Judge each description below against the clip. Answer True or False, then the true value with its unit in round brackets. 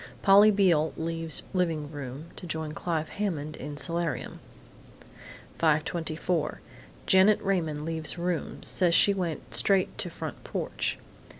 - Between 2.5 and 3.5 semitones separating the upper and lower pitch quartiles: True (2.9 semitones)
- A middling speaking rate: False (120 wpm)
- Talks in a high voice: False (165 Hz)